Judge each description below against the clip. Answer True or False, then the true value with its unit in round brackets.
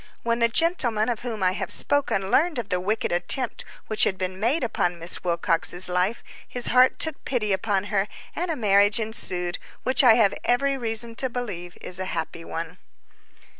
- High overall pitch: True (215 Hz)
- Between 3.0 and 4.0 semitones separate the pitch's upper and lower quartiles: False (5.0 semitones)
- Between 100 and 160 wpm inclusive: False (185 wpm)